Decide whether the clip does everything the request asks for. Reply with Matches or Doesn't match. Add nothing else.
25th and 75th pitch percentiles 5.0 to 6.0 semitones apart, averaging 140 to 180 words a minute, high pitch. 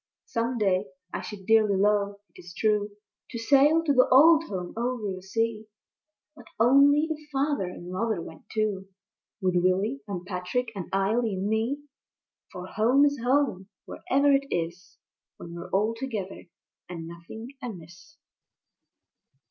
Matches